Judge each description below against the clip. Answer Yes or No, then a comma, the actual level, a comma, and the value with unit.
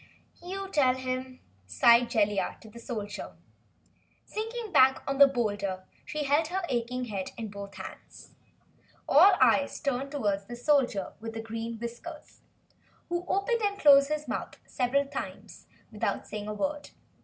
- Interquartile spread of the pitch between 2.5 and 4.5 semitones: No, average, 4.9 semitones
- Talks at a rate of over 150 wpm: No, average, 145 wpm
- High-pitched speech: Yes, very high, 255 Hz